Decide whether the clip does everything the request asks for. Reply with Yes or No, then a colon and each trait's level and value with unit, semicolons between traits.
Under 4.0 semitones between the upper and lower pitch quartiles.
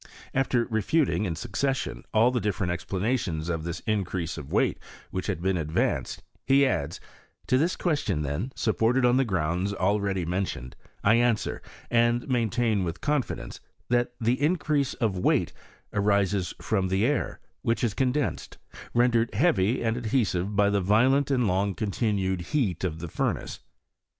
No: average, 5.0 semitones